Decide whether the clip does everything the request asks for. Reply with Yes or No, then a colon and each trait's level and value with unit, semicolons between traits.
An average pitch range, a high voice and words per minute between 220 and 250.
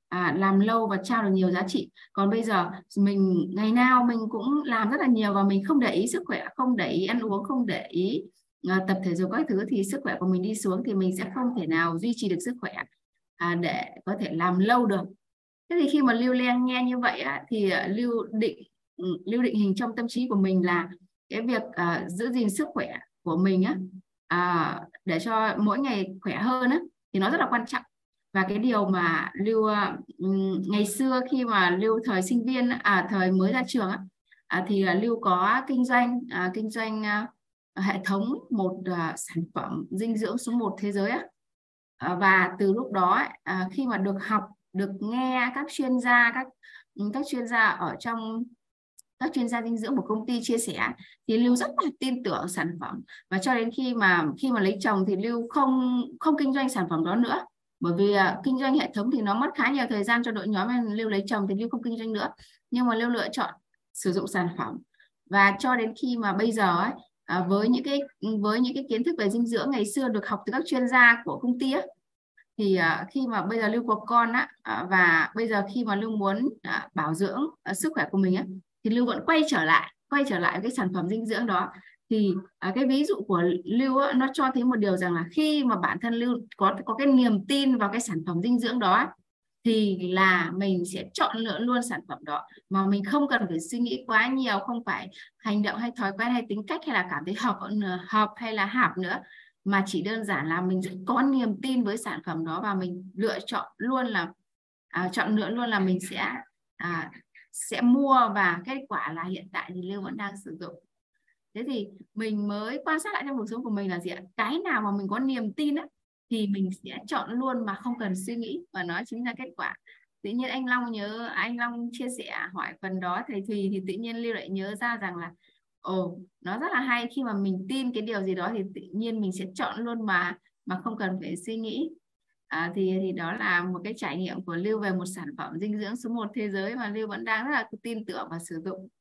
Yes: average, 4.4 semitones; high, 215 Hz; average, 235 wpm